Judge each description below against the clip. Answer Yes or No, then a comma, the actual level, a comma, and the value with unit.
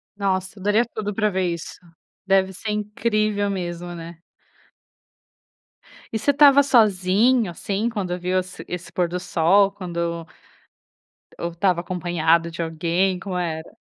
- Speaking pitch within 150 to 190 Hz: Yes, medium, 185 Hz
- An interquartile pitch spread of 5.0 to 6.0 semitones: No, average, 3.2 semitones